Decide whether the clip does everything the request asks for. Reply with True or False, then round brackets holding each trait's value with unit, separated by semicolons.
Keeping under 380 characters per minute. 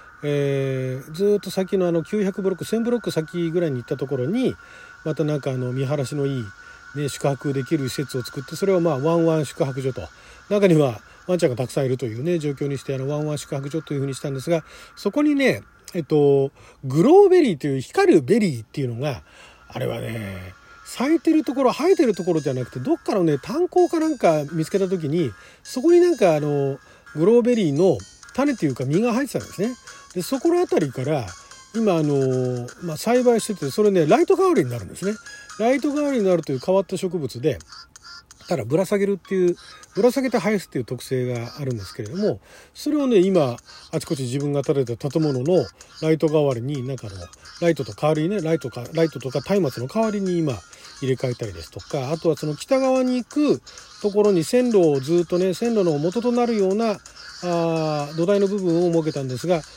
False (410 characters per minute)